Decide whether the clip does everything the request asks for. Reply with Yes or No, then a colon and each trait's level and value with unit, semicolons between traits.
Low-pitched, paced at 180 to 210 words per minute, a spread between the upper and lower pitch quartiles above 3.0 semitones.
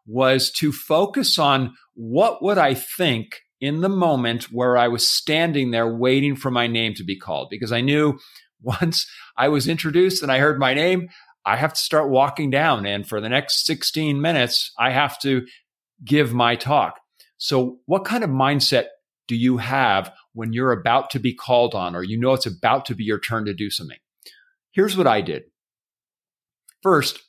Yes: low, 130 Hz; average, 185 wpm; average, 4.3 semitones